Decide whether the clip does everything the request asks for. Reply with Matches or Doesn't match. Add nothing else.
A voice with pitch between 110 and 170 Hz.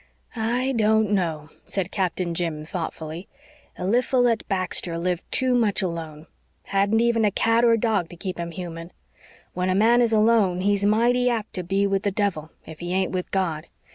Doesn't match